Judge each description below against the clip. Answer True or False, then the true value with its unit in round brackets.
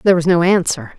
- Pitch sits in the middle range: True (180 Hz)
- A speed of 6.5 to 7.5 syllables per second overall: True (6.8 syllables/s)